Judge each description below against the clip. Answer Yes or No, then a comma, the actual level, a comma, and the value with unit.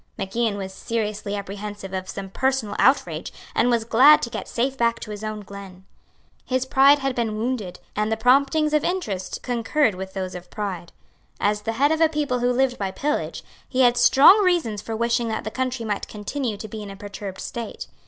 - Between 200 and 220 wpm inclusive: Yes, fast, 205 wpm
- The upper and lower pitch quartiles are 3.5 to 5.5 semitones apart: Yes, average, 4.3 semitones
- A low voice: No, high, 225 Hz